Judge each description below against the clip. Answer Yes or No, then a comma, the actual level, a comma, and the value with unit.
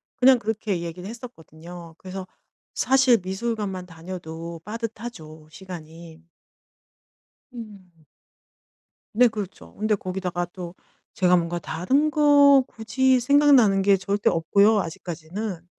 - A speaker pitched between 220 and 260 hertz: No, high, 190 Hz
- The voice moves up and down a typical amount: Yes, average, 5.0 semitones